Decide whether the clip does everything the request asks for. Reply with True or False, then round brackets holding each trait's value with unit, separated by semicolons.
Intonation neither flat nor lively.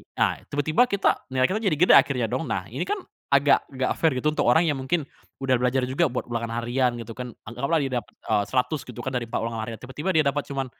True (3.7 semitones)